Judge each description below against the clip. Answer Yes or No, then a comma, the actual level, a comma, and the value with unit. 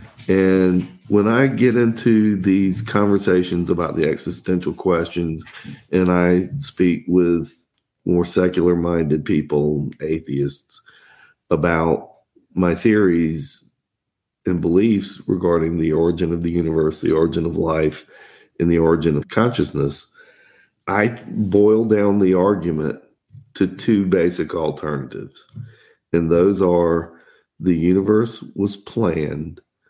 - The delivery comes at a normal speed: No, slow, 110 wpm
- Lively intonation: No, average, 3.5 semitones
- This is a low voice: Yes, very low, 90 Hz